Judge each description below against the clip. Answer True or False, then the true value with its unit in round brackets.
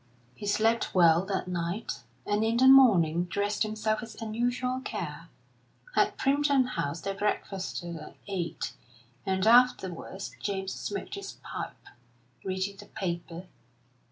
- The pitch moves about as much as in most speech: True (4.2 semitones)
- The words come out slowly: True (130 wpm)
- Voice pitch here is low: False (200 Hz)